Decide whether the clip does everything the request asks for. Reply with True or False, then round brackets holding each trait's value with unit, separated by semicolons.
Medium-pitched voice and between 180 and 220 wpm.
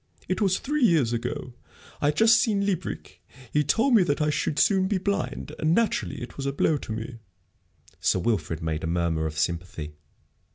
True (145 Hz; 195 wpm)